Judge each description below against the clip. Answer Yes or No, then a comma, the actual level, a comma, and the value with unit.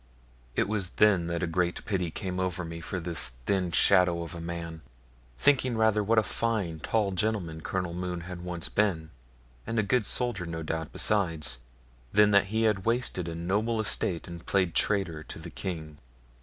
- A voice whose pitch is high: No, very low, 90 Hz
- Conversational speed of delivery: Yes, average, 180 wpm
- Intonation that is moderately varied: Yes, average, 3.9 semitones